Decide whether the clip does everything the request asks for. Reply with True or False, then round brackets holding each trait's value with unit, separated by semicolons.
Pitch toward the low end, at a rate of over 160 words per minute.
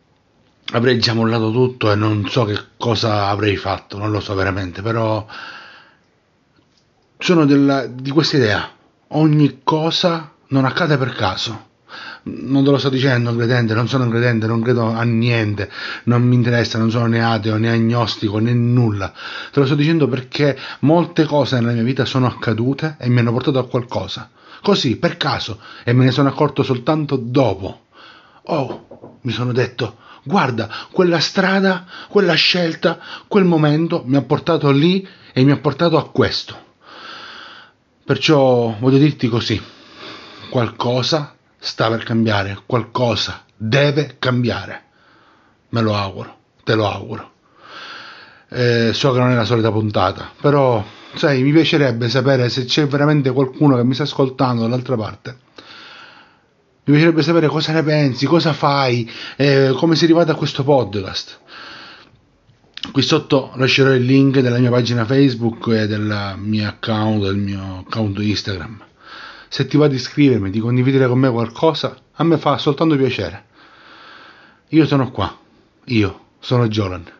False (125 Hz; 150 wpm)